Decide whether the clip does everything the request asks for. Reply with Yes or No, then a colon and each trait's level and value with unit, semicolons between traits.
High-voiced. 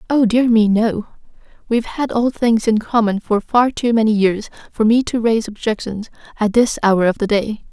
Yes: high, 220 Hz